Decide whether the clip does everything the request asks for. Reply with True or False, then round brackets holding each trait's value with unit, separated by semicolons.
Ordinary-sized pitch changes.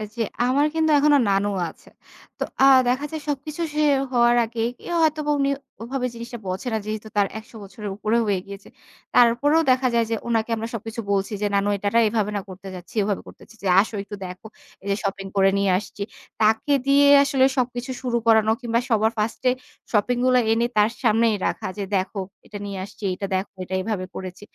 True (3.8 semitones)